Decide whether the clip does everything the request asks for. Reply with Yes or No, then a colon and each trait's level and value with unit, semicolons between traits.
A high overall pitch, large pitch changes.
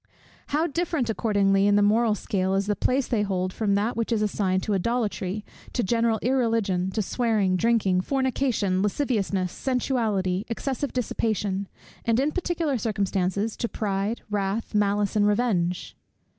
No: high, 210 Hz; average, 3.4 semitones